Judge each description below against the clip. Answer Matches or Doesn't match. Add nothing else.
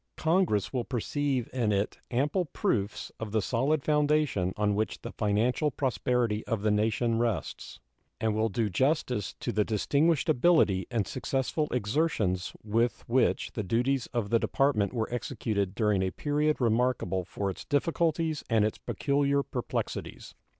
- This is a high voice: Doesn't match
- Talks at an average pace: Matches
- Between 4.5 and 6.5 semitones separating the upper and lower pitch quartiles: Matches